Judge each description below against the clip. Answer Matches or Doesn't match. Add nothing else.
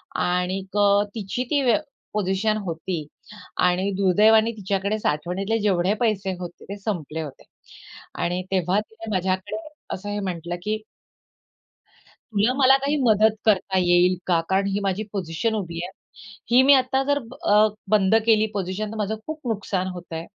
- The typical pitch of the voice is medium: Doesn't match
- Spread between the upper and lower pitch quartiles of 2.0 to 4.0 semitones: Matches